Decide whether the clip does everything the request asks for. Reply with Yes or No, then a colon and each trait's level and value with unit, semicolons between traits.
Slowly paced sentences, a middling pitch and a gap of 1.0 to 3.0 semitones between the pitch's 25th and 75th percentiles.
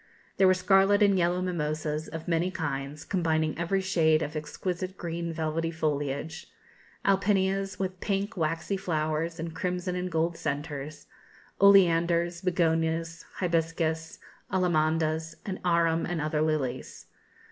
Yes: slow, 125 wpm; medium, 165 Hz; narrow, 2.6 semitones